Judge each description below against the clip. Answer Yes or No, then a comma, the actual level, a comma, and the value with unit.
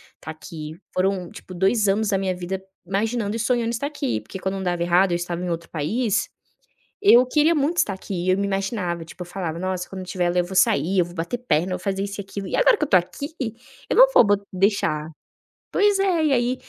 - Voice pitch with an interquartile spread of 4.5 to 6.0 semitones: Yes, average, 4.8 semitones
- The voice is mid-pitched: No, high, 195 Hz